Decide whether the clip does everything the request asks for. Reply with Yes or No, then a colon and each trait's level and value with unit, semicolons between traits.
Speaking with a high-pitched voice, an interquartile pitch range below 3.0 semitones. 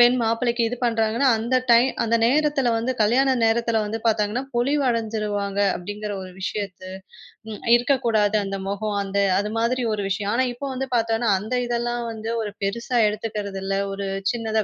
Yes: high, 225 Hz; narrow, 2.6 semitones